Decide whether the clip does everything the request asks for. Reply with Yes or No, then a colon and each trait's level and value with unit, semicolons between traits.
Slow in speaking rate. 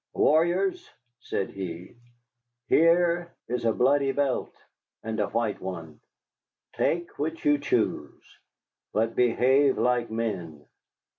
Yes: slow, 105 wpm